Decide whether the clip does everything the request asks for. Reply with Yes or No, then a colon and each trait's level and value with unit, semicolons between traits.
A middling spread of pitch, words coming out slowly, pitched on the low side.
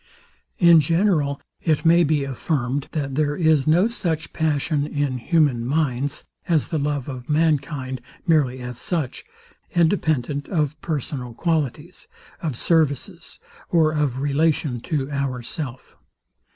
No: average, 3.1 semitones; slow, 125 wpm; medium, 150 Hz